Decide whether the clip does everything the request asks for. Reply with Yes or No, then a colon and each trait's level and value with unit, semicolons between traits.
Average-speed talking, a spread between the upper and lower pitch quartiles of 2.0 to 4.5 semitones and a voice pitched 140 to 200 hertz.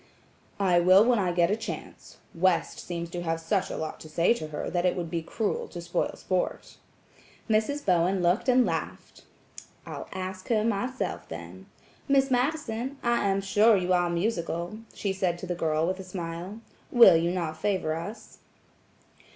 Yes: average, 175 wpm; average, 4.1 semitones; medium, 185 Hz